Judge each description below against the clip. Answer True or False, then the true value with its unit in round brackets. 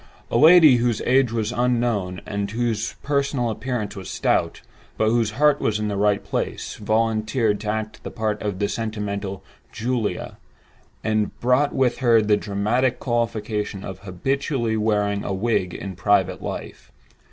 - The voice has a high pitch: False (110 Hz)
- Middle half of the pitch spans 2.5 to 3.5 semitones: True (2.8 semitones)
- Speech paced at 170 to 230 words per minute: False (145 wpm)